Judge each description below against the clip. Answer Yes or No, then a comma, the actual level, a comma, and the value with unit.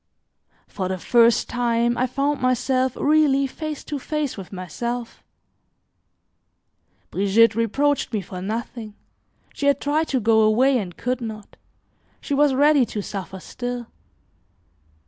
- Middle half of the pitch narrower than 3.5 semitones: No, average, 4.2 semitones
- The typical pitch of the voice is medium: No, high, 245 Hz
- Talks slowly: Yes, slow, 130 wpm